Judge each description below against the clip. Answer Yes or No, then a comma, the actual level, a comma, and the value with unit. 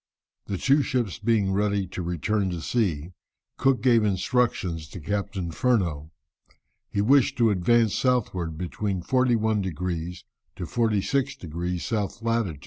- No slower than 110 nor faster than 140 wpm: Yes, slow, 135 wpm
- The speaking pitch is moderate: No, low, 100 Hz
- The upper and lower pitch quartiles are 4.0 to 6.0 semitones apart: Yes, average, 5.0 semitones